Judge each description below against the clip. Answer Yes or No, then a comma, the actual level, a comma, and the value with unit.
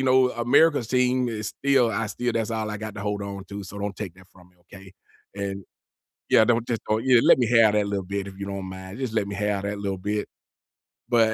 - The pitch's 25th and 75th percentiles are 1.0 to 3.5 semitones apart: Yes, average, 3.0 semitones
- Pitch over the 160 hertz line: No, low, 105 Hz